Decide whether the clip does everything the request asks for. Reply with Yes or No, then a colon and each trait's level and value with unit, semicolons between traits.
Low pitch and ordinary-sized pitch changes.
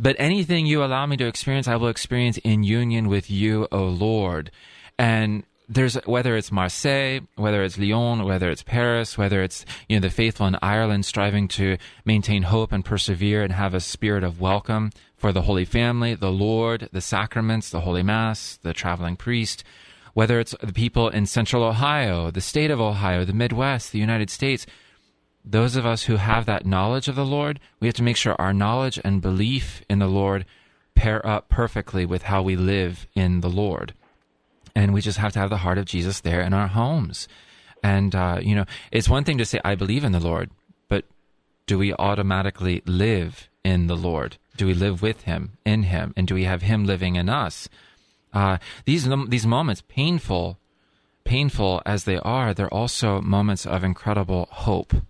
Yes: low, 105 Hz; average, 3.6 semitones